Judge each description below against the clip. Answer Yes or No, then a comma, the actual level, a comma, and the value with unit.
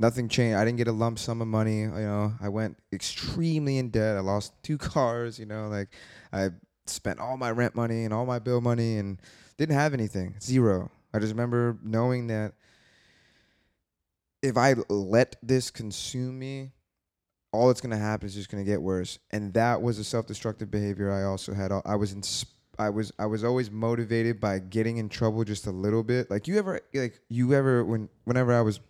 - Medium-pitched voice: No, low, 115 Hz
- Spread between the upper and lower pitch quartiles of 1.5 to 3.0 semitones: Yes, narrow, 2.6 semitones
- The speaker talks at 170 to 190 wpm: No, fast, 205 wpm